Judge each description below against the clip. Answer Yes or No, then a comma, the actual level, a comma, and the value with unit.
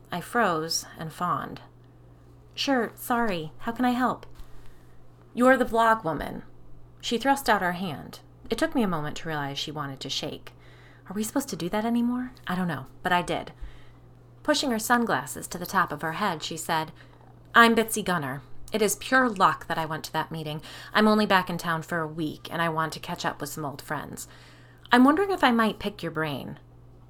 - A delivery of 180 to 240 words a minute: Yes, fast, 205 wpm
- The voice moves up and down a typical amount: No, wide, 7.2 semitones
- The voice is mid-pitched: Yes, medium, 170 Hz